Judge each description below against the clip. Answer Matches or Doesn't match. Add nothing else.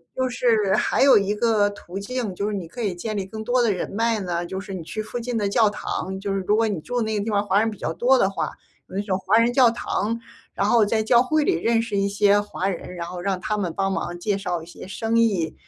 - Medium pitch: Doesn't match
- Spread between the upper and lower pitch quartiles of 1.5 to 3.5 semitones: Matches